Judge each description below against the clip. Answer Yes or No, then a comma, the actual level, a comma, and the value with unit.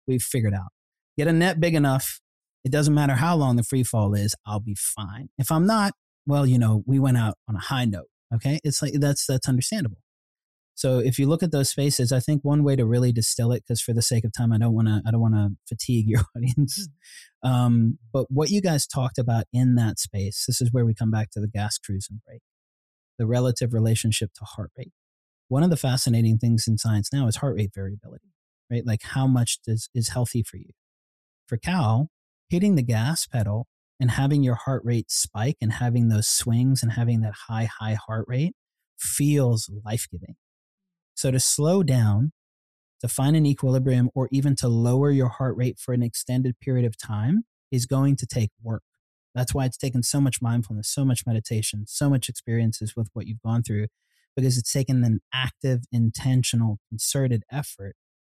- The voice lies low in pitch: Yes, low, 120 Hz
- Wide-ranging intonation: No, average, 3.4 semitones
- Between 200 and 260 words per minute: Yes, fast, 205 wpm